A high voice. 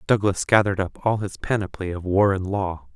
No: low, 100 Hz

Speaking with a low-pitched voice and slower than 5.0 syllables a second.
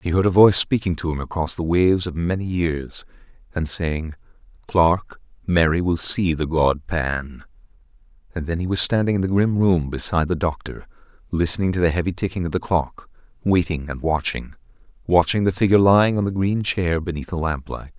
No: very low, 85 Hz; 5.5 syllables/s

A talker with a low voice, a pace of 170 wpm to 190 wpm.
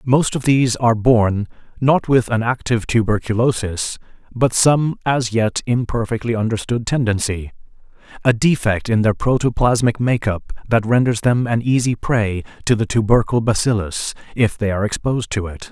No: low, 115 Hz; average, 150 wpm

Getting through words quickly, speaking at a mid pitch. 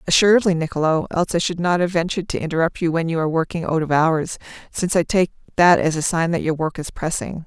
Yes: fast, 240 wpm; medium, 165 Hz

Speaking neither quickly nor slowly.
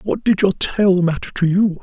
No: fast, 230 wpm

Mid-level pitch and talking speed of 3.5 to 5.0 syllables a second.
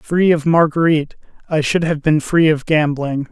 Yes: medium, 155 Hz; 4.7 syllables/s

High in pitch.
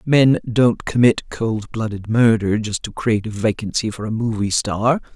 No: low, 110 Hz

